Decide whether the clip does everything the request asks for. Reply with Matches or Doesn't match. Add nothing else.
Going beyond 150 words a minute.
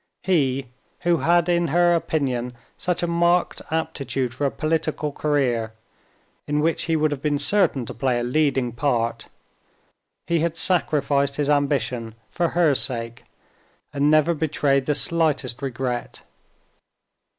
Doesn't match